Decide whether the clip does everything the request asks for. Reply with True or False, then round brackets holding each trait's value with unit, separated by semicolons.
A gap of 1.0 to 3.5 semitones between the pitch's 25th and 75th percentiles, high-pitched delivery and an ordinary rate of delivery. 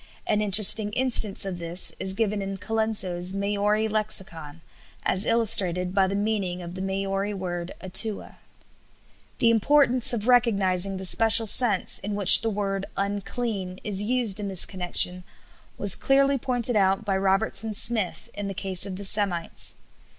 True (2.5 semitones; 200 Hz; 150 wpm)